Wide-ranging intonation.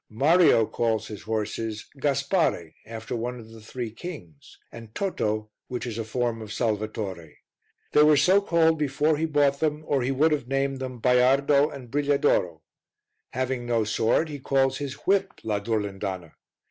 No: average, 4.7 semitones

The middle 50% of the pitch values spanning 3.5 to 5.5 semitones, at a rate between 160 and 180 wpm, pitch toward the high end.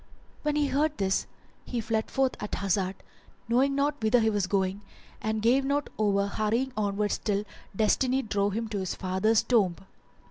Yes: average, 4.6 semitones; average, 170 wpm; high, 220 Hz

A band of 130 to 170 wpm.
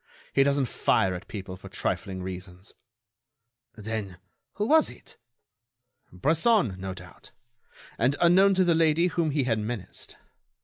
Yes: slow, 135 wpm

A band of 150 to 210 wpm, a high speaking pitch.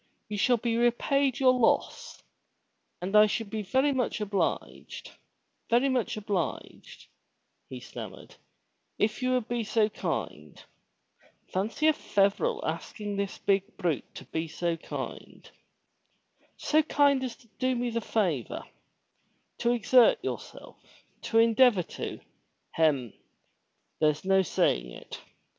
No: slow, 135 wpm; high, 225 Hz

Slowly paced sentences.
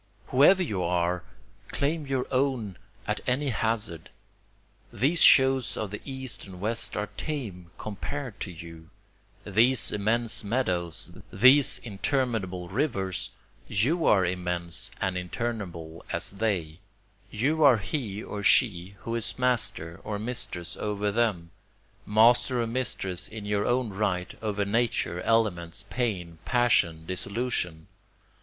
Yes: slow, 125 wpm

